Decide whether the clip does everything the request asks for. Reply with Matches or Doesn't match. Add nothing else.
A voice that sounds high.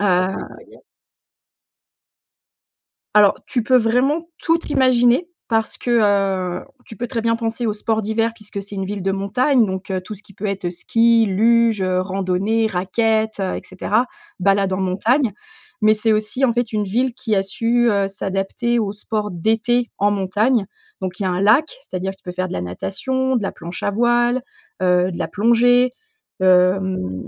Matches